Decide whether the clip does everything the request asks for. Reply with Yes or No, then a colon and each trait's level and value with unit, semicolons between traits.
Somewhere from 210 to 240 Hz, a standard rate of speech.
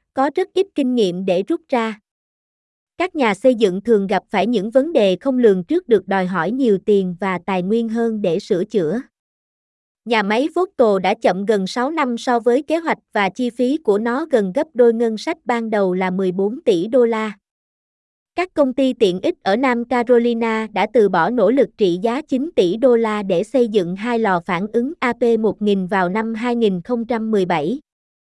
Yes: high, 230 Hz; average, 195 wpm